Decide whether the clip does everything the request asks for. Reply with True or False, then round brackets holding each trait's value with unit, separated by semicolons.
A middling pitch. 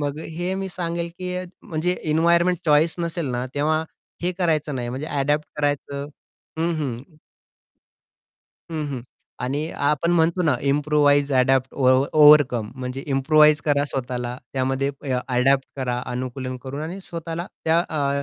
True (145 Hz)